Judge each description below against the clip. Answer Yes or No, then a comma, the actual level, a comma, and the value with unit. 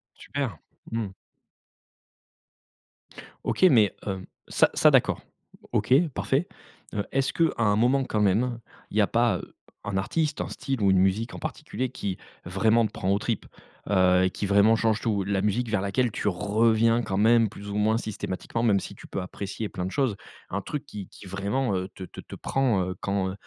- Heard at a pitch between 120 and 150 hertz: No, low, 105 Hz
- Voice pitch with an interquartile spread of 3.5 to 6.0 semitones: No, average, 3.1 semitones